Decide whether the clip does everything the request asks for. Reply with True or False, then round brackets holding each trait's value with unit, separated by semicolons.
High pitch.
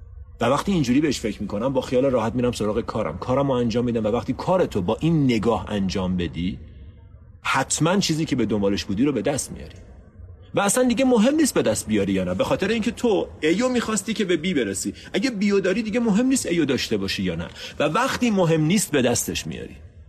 False (120 Hz)